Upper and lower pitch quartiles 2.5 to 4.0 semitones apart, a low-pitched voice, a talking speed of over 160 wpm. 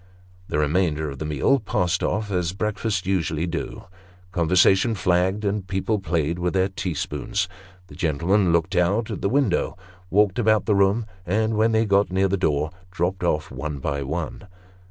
Yes: average, 3.6 semitones; very low, 95 Hz; average, 175 wpm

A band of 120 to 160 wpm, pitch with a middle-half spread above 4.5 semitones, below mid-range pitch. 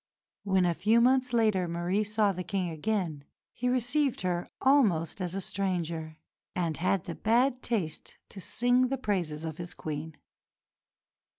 No: average, 155 wpm; wide, 5.6 semitones; high, 190 Hz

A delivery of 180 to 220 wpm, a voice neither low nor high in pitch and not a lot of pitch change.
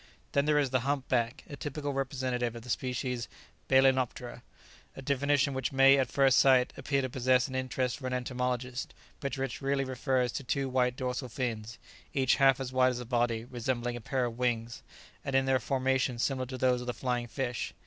No: average, 200 wpm; low, 130 Hz; narrow, 1.6 semitones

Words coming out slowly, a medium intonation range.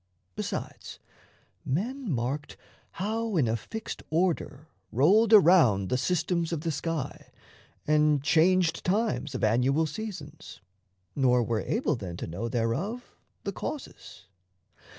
No: slow, 120 wpm; wide, 6.8 semitones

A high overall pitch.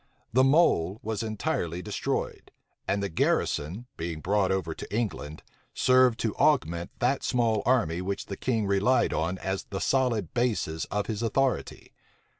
No: low, 105 Hz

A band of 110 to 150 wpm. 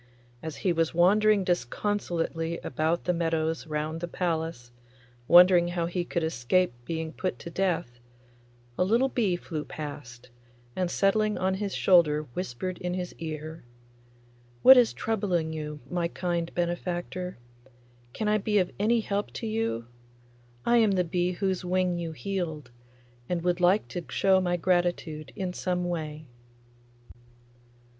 Yes: average, 145 wpm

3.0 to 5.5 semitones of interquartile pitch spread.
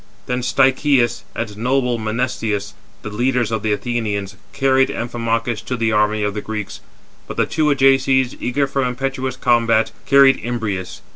Yes: average, 3.4 semitones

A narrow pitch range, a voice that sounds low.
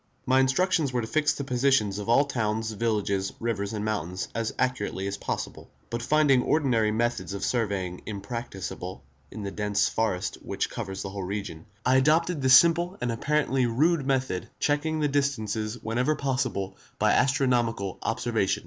No: average, 5.0 semitones; low, 115 Hz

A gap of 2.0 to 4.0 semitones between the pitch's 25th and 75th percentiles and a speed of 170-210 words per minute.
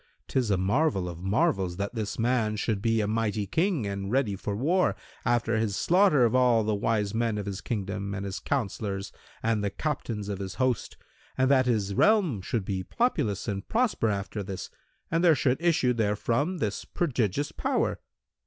No: average, 4.6 semitones; average, 180 wpm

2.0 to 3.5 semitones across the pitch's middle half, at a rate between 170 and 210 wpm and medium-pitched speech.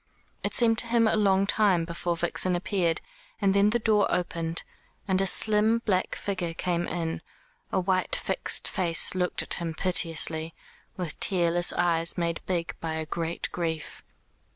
No: average, 2.9 semitones; average, 160 wpm; medium, 175 Hz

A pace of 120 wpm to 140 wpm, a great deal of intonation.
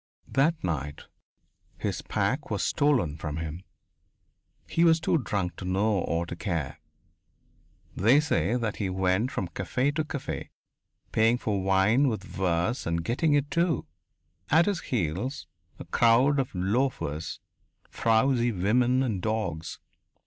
Yes: slow, 135 wpm; wide, 6.7 semitones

